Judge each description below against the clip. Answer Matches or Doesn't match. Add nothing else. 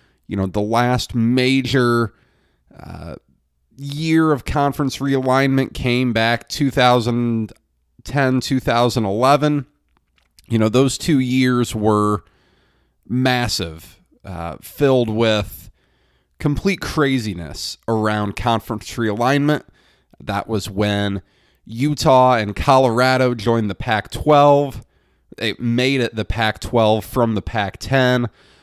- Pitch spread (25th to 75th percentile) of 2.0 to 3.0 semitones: Doesn't match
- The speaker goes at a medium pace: Doesn't match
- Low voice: Matches